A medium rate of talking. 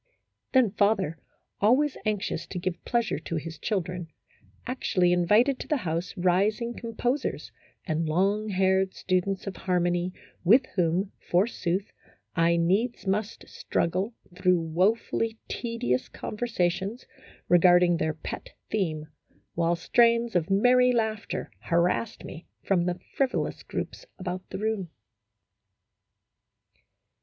No: slow, 115 wpm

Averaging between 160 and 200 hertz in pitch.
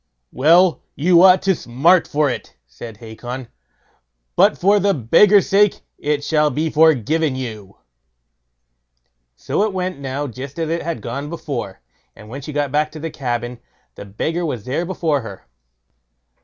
No: medium, 145 Hz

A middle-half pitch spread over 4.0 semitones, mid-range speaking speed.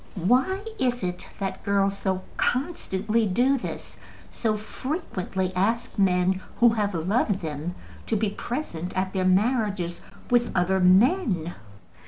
No: average, 4.5 semitones; slow, 130 wpm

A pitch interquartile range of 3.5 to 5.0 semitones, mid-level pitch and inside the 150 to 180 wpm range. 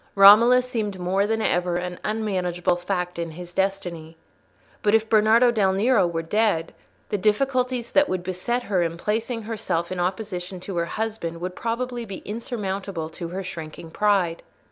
No: average, 4.0 semitones; high, 195 Hz; average, 165 wpm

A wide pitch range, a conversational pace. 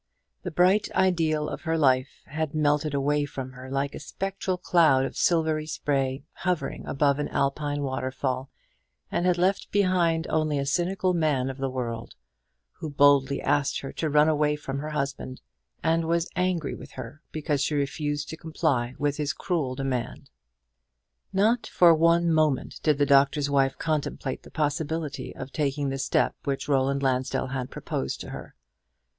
No: average, 2.9 semitones; average, 165 wpm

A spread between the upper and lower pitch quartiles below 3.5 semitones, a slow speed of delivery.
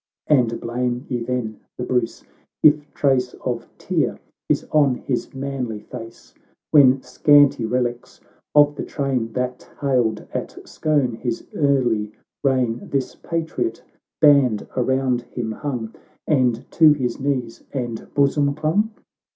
Yes: average, 2.9 semitones; slow, 125 wpm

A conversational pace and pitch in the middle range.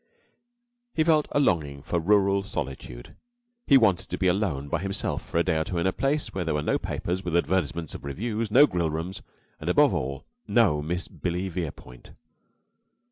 No: average, 190 wpm; very low, 90 Hz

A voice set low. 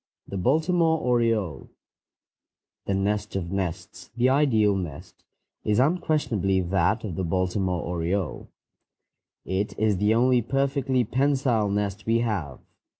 Yes: low, 105 Hz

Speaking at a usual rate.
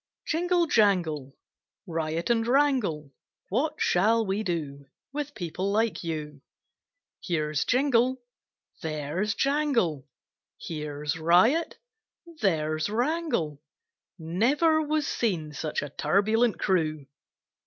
No: slow, 95 wpm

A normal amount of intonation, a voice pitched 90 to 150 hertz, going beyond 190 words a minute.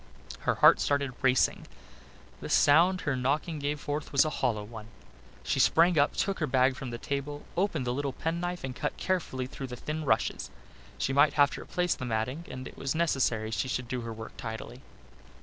Yes: average, 3.5 semitones; medium, 140 Hz; average, 200 wpm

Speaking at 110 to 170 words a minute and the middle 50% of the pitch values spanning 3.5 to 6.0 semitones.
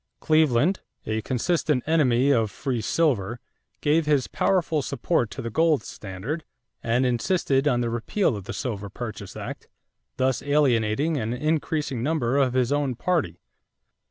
Yes: average, 145 wpm; average, 4.7 semitones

